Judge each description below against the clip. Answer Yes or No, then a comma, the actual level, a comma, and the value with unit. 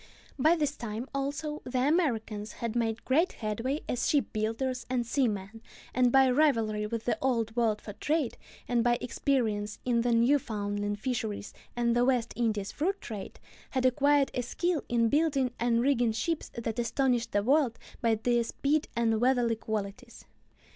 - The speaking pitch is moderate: No, high, 240 Hz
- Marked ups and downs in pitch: No, average, 3.2 semitones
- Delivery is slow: No, average, 160 wpm